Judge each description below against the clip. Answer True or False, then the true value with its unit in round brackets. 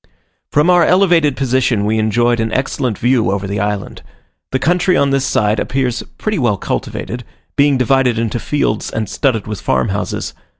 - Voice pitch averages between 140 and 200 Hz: False (125 Hz)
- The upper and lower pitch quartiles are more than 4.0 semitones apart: True (4.4 semitones)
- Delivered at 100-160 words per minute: False (170 wpm)